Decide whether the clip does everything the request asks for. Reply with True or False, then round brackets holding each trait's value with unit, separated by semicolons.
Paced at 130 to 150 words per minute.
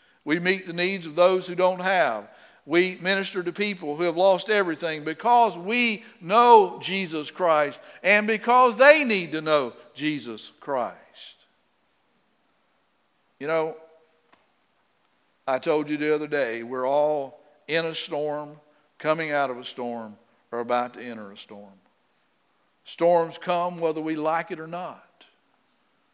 True (140 wpm)